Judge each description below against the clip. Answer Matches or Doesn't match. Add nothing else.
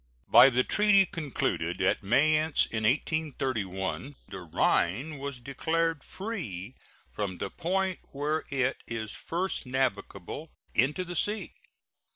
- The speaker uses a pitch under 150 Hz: Matches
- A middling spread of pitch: Doesn't match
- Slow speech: Matches